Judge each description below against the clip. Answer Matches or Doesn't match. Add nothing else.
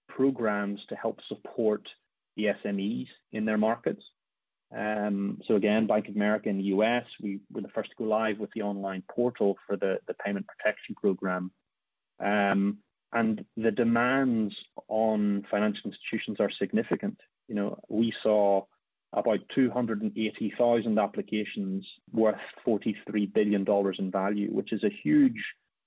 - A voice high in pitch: Doesn't match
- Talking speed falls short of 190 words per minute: Matches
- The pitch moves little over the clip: Matches